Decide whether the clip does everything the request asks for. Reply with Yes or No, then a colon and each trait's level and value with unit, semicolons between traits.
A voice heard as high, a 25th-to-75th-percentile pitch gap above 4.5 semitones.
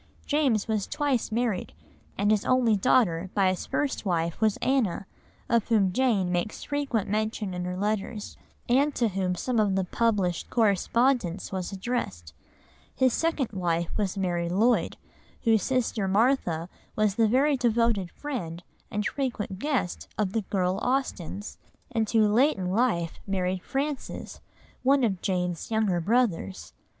Yes: high, 210 Hz; average, 5.0 semitones